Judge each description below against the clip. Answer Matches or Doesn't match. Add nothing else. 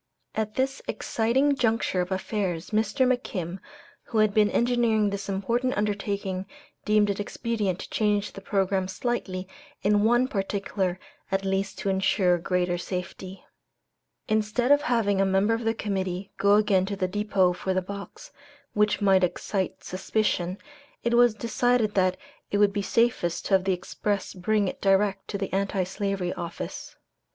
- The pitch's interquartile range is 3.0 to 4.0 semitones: Doesn't match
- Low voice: Doesn't match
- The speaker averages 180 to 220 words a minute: Doesn't match